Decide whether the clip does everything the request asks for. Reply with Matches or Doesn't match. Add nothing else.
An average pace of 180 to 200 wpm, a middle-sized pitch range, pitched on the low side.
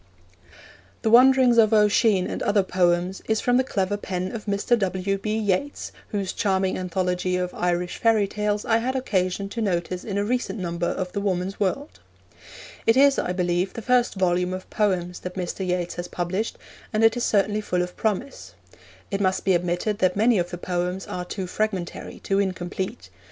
Doesn't match